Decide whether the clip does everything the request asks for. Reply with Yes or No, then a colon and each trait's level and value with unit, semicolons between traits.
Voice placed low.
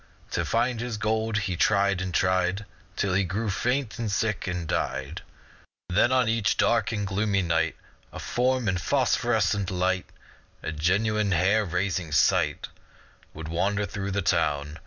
Yes: low, 100 Hz